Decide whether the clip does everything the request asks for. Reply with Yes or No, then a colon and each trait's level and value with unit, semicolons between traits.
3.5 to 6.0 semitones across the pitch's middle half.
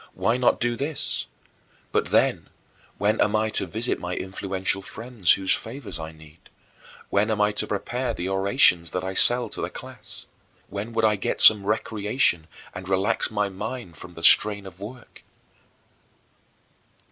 No: average, 3.1 semitones